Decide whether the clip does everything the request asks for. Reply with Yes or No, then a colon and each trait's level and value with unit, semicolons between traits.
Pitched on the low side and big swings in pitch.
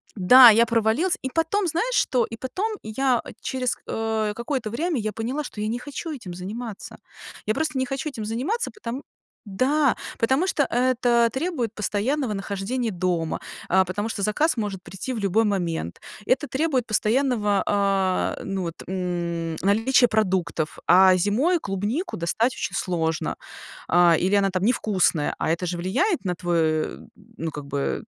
No: high, 220 Hz; wide, 5.7 semitones